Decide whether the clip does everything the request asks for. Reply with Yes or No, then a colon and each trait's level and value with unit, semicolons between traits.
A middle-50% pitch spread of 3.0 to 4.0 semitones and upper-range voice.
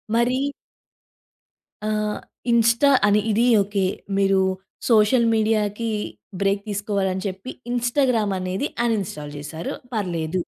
Yes: average, 3.3 semitones; high, 210 Hz